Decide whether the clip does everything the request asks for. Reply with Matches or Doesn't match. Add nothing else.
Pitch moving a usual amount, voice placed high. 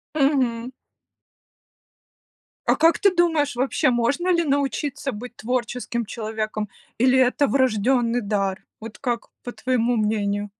Matches